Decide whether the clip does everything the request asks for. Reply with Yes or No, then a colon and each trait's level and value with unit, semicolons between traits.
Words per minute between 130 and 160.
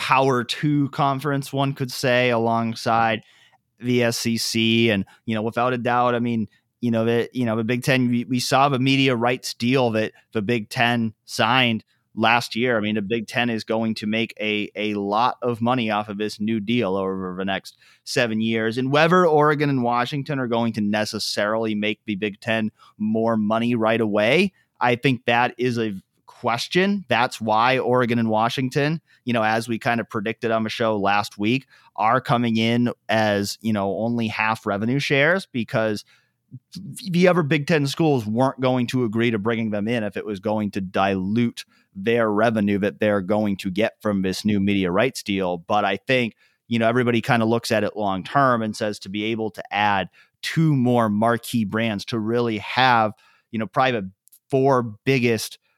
No: average, 190 wpm